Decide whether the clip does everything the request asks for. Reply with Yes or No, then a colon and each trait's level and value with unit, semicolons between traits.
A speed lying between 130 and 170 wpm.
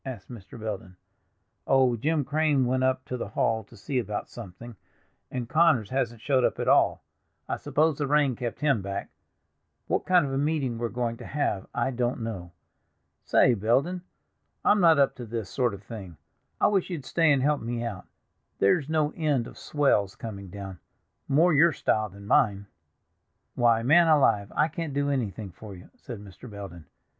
No: average, 180 wpm